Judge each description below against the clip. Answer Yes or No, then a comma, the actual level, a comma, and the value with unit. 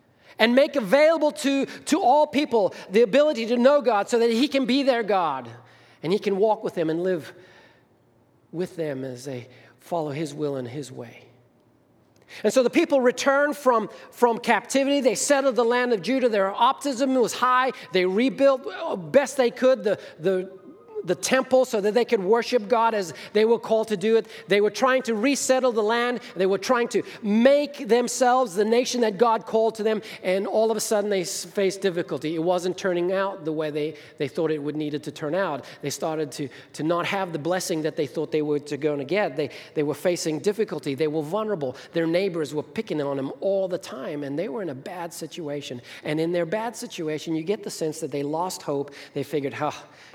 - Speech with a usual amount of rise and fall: No, wide, 7.4 semitones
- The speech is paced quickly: Yes, fast, 215 wpm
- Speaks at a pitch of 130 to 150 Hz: No, high, 200 Hz